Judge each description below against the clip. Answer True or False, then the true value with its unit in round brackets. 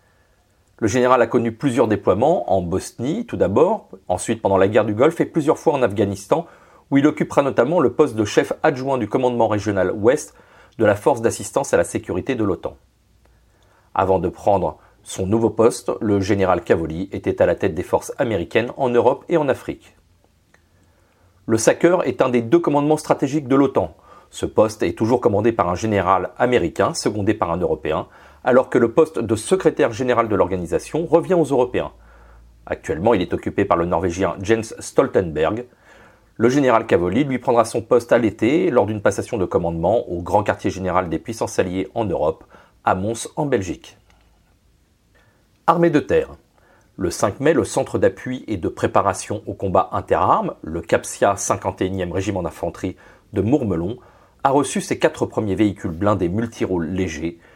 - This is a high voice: False (105 Hz)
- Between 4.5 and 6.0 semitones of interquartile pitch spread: True (5.4 semitones)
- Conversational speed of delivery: True (175 wpm)